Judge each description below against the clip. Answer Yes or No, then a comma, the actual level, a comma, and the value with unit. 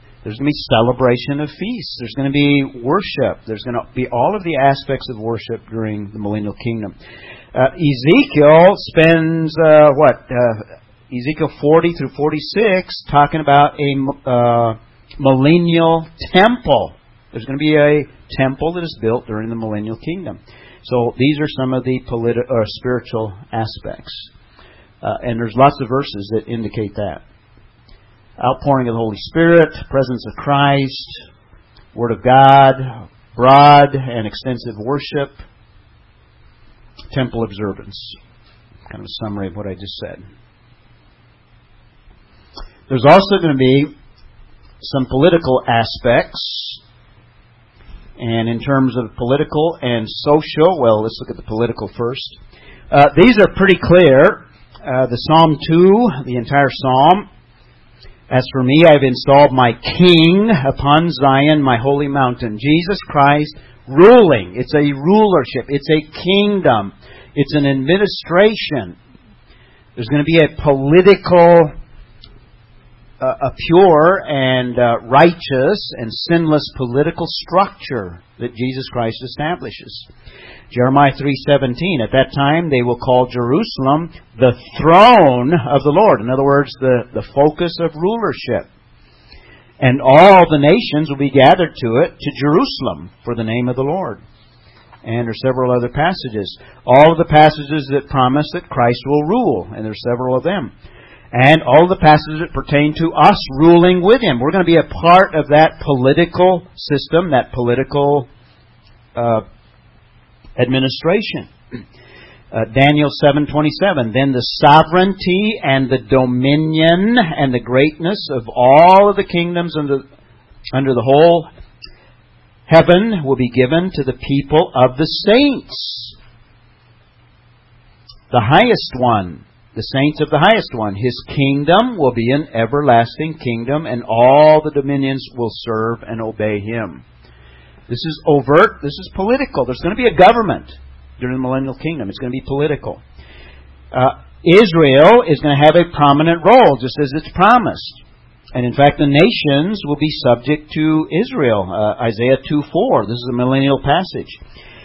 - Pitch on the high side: No, low, 135 Hz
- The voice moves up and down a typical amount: Yes, average, 4.5 semitones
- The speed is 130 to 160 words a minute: Yes, average, 145 wpm